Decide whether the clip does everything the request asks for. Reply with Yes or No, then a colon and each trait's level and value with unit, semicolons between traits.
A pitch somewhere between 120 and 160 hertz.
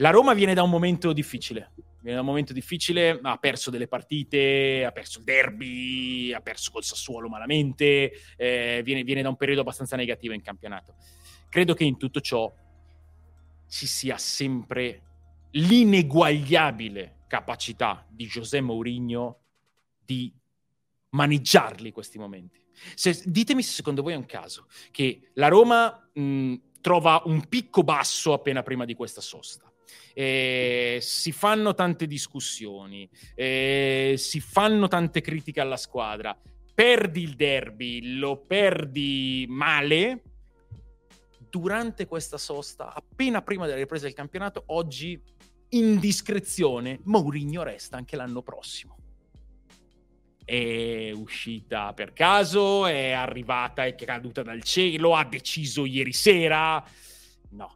Yes: low, 135 Hz